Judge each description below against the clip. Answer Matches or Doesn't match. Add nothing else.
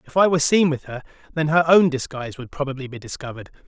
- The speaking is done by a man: Matches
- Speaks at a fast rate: Matches